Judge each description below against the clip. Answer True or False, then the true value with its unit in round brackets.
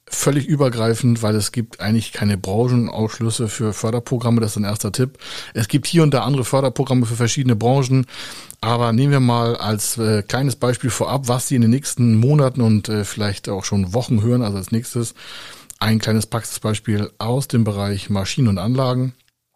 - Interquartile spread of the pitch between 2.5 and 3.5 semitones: True (2.9 semitones)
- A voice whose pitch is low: True (120 Hz)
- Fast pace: False (180 wpm)